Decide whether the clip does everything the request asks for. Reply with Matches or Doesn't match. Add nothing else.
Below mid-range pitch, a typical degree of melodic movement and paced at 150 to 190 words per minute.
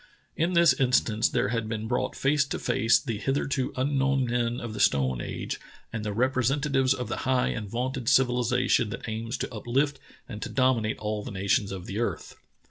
Doesn't match